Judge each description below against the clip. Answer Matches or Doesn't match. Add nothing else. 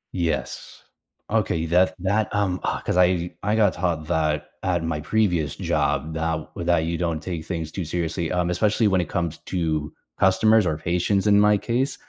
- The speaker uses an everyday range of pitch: Matches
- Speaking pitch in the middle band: Doesn't match